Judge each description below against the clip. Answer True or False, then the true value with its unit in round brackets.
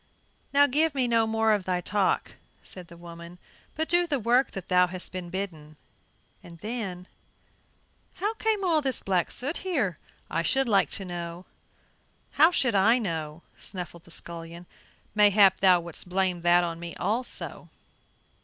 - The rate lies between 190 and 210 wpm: False (155 wpm)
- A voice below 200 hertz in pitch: True (190 Hz)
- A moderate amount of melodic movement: False (6.2 semitones)